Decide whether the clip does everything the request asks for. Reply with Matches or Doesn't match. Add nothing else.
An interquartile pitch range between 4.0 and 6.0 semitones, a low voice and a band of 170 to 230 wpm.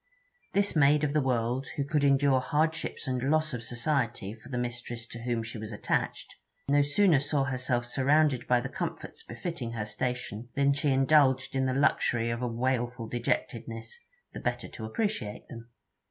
Doesn't match